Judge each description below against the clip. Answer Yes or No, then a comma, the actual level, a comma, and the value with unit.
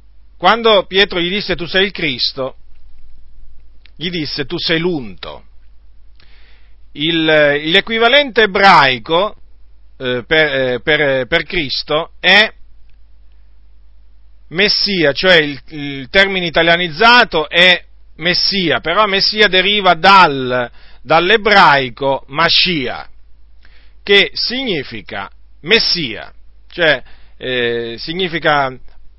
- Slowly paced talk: Yes, slow, 85 wpm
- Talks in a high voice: No, medium, 140 Hz